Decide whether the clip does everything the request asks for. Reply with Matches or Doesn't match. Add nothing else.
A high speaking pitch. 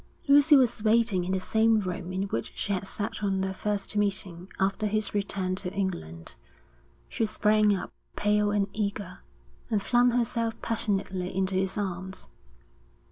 Matches